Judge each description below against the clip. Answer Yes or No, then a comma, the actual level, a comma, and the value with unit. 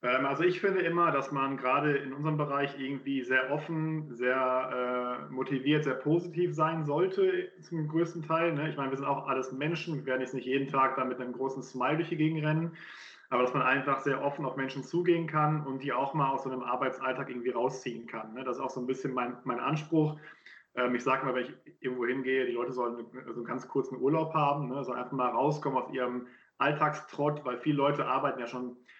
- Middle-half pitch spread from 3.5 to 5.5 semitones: No, average, 3.1 semitones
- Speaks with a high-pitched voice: No, low, 135 Hz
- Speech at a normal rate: No, fast, 230 wpm